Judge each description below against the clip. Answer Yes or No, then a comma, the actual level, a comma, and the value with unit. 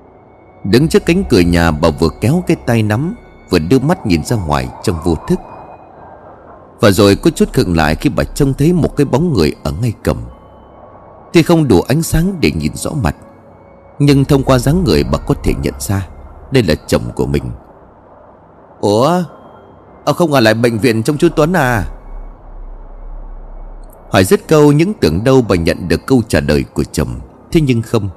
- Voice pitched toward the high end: No, low, 115 Hz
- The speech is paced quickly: No, average, 190 wpm